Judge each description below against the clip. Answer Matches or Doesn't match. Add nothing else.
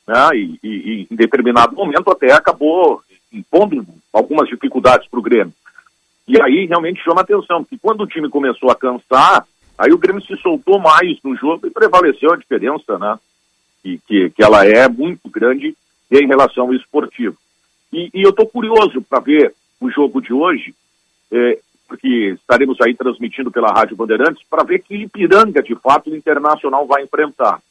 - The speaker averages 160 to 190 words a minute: Matches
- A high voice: Doesn't match